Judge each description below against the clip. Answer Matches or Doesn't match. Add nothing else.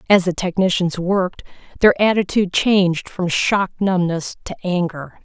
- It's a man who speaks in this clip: Doesn't match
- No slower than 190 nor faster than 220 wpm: Doesn't match